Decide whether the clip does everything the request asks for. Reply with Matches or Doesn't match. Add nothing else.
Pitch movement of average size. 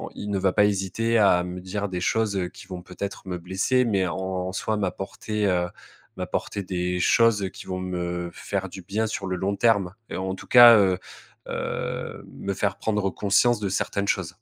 Doesn't match